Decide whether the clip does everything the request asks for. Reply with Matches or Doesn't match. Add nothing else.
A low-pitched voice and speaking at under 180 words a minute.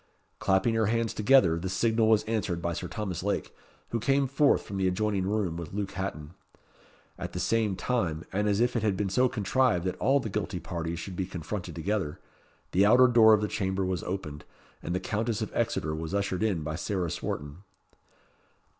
Doesn't match